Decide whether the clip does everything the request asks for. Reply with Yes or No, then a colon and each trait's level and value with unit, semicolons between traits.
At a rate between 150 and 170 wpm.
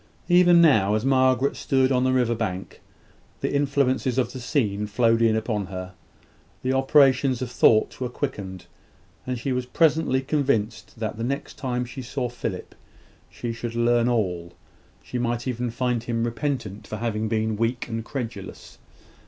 Yes: average, 160 wpm